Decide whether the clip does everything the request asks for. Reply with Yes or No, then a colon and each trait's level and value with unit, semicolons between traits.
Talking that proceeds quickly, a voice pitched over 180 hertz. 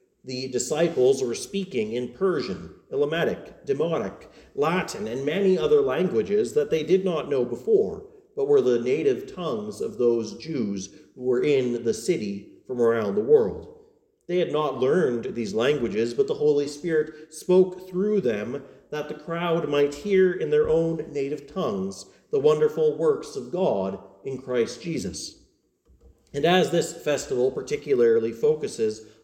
No: average, 150 wpm; high, 190 Hz